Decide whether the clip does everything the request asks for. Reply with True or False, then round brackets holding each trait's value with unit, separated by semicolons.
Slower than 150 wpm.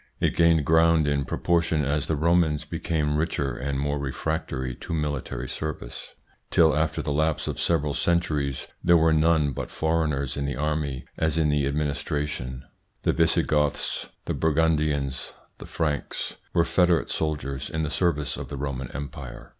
False (160 wpm)